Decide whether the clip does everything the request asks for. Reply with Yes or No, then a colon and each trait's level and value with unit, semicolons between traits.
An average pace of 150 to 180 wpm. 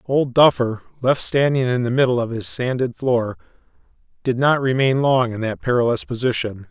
Yes: average, 170 wpm